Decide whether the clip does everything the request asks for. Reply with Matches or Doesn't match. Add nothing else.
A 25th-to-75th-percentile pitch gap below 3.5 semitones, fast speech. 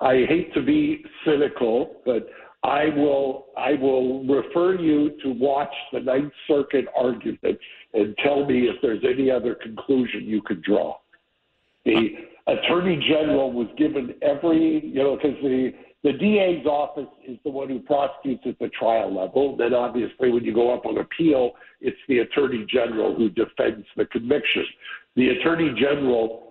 Doesn't match